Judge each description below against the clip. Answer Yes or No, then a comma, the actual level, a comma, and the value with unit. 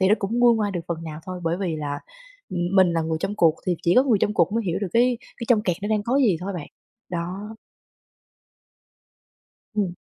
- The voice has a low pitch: No, high, 195 Hz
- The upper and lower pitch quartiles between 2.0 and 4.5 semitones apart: Yes, average, 3.9 semitones